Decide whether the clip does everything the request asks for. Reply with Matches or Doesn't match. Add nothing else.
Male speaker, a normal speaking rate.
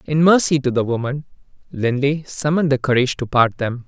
Matches